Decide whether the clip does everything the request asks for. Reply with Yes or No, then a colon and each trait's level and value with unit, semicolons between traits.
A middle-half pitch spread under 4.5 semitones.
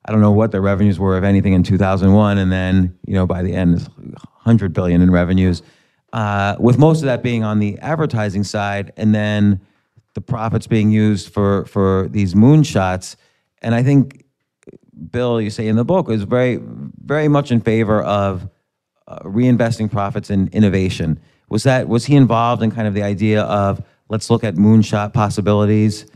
Yes: average, 2.8 semitones